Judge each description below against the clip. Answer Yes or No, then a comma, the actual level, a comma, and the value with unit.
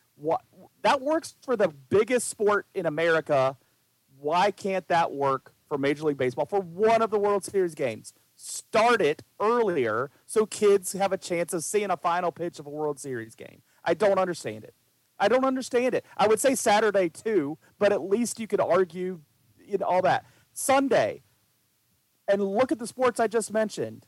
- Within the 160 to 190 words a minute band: Yes, average, 185 wpm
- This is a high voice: Yes, high, 195 Hz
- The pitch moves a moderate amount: No, wide, 5.9 semitones